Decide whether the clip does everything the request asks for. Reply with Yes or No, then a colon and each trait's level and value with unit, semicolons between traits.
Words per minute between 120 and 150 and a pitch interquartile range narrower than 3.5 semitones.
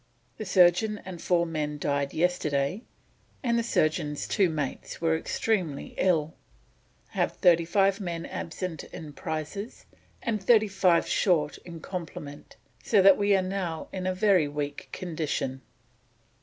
No: average, 140 wpm; average, 3.9 semitones